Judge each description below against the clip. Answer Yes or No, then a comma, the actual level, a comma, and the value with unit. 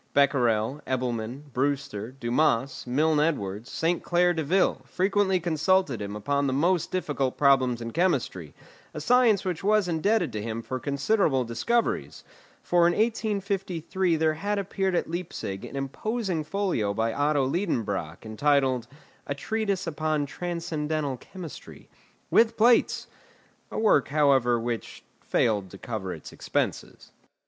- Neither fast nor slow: No, slow, 130 wpm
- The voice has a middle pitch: Yes, medium, 150 Hz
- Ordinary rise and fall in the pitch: No, wide, 6.9 semitones